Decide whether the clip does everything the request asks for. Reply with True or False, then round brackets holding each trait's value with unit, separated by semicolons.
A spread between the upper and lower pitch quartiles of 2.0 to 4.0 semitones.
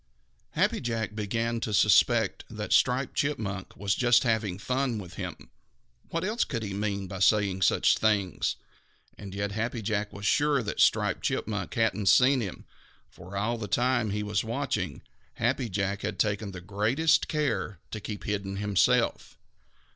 True (2.9 semitones)